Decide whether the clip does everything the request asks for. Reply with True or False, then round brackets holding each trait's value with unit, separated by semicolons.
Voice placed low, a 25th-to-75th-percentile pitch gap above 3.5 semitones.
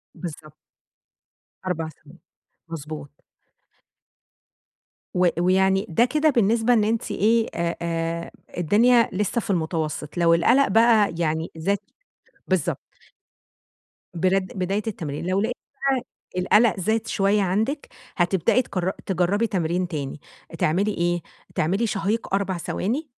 False (190 Hz; 4.7 semitones)